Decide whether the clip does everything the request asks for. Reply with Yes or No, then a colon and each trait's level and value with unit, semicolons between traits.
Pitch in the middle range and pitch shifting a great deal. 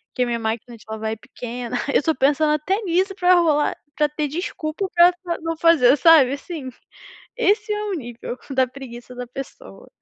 No: very high, 300 Hz; wide, 5.9 semitones